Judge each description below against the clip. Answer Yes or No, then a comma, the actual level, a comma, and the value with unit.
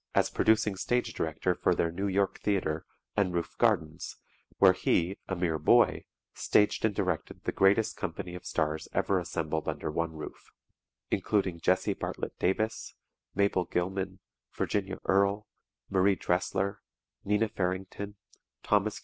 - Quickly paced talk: No, average, 140 wpm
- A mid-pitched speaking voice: No, very low, 95 Hz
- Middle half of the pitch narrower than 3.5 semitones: Yes, average, 2.7 semitones